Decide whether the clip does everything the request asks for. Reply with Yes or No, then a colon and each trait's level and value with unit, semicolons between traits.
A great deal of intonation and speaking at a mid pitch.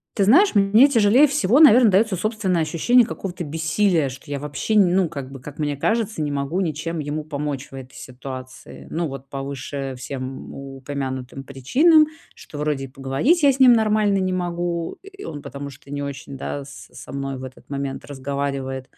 Yes: wide, 6.6 semitones; medium, 150 Hz